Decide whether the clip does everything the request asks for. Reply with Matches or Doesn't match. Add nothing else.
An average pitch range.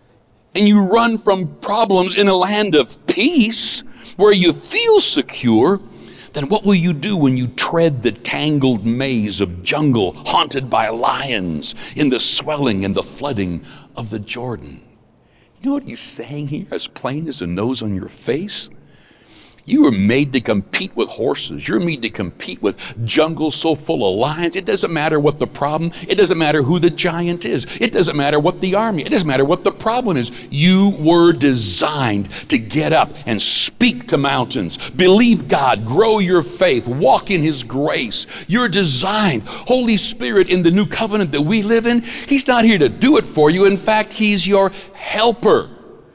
Doesn't match